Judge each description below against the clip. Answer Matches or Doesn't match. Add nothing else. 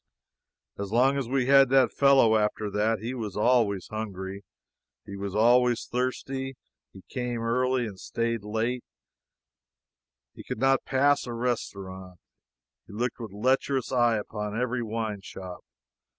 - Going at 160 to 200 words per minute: Doesn't match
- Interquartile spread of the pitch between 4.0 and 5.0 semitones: Doesn't match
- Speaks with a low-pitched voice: Matches